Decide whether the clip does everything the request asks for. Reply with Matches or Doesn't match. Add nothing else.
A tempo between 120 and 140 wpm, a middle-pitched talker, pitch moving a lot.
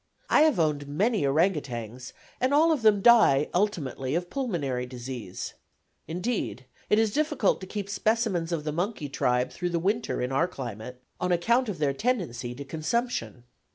Doesn't match